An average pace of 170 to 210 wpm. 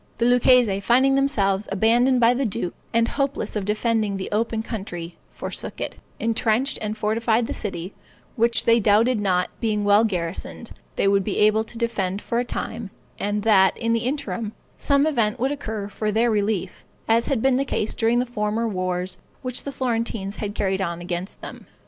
Yes: average, 185 wpm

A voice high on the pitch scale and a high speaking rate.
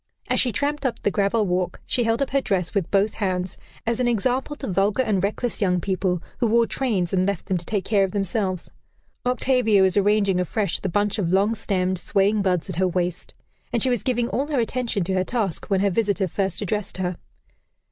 Yes: high, 200 Hz; fast, 220 wpm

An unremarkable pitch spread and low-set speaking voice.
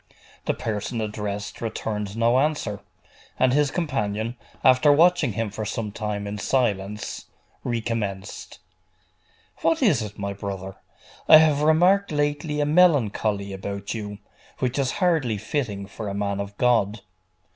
No: wide, 6.1 semitones; low, 110 Hz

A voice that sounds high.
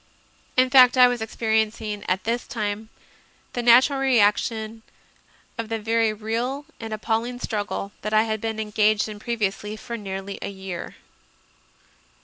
Yes: high, 220 Hz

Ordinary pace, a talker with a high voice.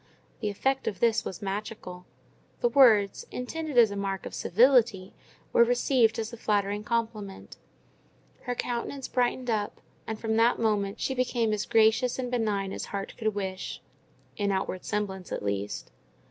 Yes: average, 155 wpm; high, 220 Hz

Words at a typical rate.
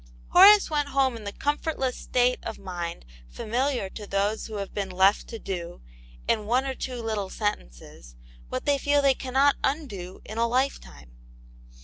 Yes: average, 165 wpm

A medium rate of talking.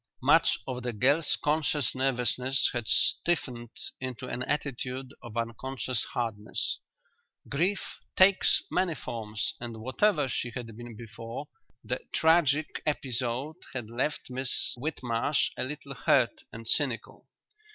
No: slow, 120 wpm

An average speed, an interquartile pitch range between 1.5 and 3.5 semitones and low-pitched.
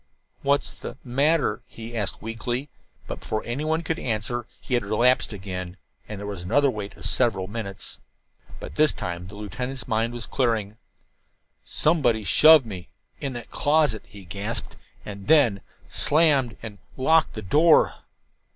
No: average, 150 wpm; average, 5.3 semitones; low, 115 Hz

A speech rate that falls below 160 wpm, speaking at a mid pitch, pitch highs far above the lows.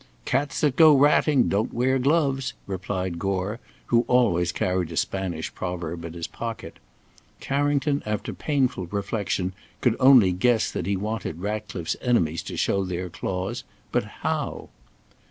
No: average, 140 wpm; low, 100 Hz; wide, 6.1 semitones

